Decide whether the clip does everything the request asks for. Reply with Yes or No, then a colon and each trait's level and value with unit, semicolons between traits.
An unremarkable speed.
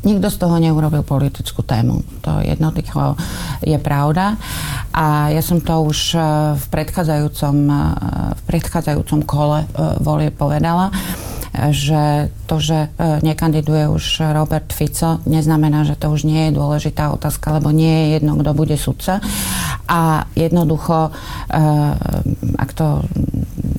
Yes: average, 120 wpm